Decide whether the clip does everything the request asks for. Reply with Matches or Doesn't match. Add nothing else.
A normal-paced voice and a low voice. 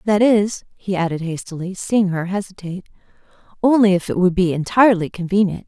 Doesn't match